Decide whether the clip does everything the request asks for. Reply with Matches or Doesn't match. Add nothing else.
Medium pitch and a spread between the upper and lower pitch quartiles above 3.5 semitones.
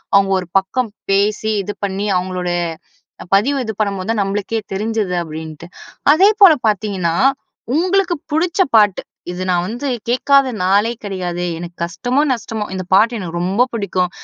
Doesn't match